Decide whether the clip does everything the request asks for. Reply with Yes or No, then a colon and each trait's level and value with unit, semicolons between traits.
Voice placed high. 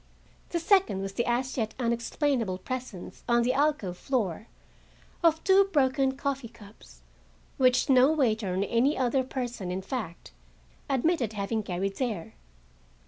Yes: high, 245 Hz